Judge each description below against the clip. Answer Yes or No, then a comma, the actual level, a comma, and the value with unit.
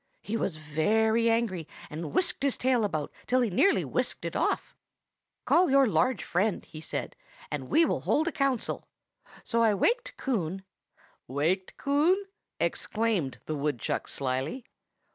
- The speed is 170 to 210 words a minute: No, average, 145 wpm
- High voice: Yes, high, 220 Hz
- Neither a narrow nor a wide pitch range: No, wide, 8.8 semitones